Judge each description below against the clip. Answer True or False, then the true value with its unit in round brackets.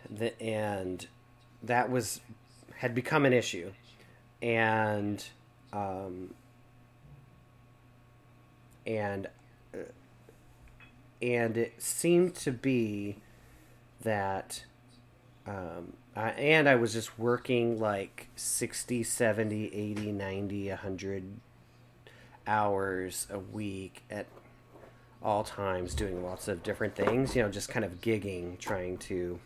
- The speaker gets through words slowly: True (100 wpm)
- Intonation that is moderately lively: True (3.0 semitones)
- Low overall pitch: True (115 Hz)